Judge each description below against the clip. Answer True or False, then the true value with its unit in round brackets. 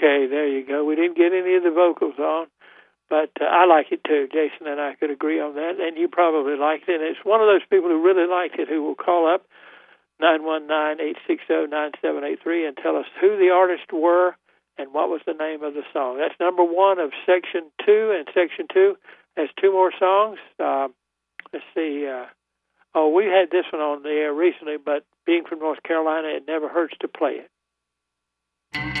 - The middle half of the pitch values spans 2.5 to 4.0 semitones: True (3.3 semitones)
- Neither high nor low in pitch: True (160 Hz)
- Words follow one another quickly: True (220 wpm)